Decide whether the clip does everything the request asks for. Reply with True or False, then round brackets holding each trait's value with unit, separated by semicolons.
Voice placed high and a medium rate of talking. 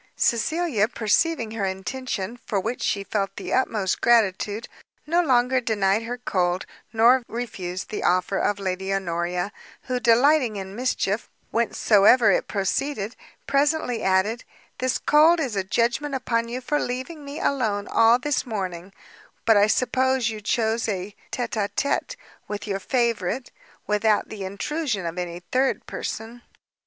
True (225 Hz; 145 wpm)